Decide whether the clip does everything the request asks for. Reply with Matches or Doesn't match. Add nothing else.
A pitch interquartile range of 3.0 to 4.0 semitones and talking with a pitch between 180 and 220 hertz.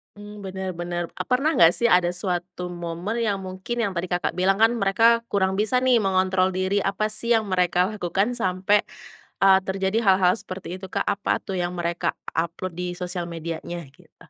Doesn't match